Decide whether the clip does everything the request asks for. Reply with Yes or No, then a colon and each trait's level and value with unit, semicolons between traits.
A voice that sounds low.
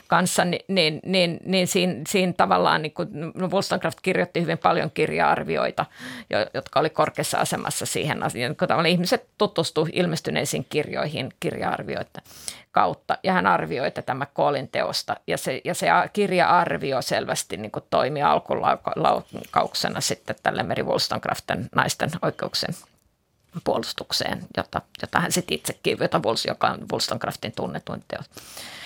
No: medium, 175 Hz